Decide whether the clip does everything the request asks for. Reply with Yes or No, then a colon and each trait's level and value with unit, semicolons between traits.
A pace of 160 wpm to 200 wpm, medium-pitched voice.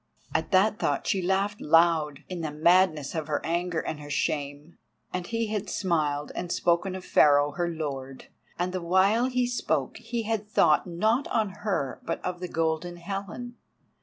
Yes: average, 170 wpm; medium, 175 Hz